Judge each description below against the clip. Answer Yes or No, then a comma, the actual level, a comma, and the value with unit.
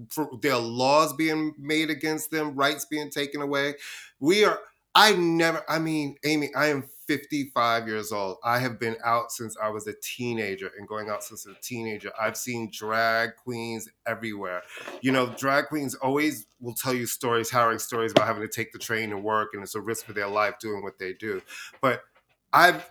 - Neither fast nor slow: Yes, average, 195 wpm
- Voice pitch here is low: Yes, low, 120 Hz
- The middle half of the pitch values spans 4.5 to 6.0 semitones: Yes, average, 4.9 semitones